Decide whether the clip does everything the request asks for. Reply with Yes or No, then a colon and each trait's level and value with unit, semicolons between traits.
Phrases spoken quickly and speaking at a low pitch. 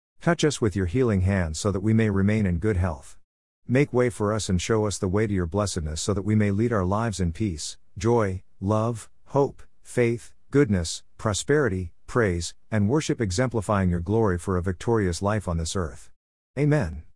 No: average, 190 wpm; low, 100 Hz